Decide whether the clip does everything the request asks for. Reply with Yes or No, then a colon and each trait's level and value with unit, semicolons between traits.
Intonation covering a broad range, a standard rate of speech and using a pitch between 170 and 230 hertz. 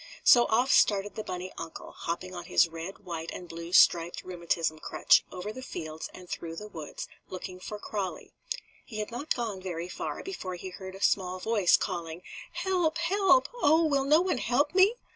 Yes: wide, 6.3 semitones; average, 185 wpm; high, 190 Hz